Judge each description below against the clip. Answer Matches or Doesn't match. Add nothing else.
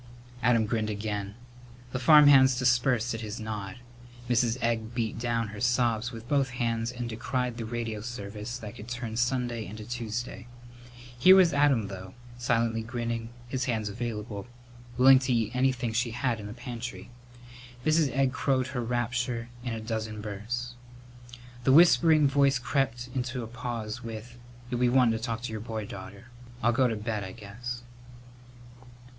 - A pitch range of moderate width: Doesn't match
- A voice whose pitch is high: Doesn't match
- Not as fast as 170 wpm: Matches